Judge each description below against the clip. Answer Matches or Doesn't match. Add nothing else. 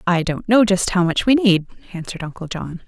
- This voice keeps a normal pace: Doesn't match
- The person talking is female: Matches